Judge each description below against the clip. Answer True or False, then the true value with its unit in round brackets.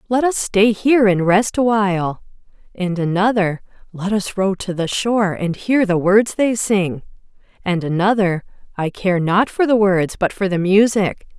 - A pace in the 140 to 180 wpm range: True (175 wpm)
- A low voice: False (195 Hz)